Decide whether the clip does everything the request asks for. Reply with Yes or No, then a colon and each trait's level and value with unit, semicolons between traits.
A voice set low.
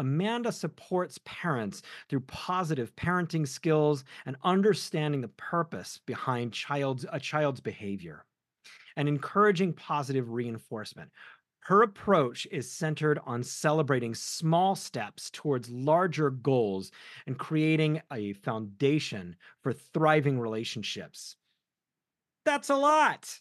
No: medium, 150 Hz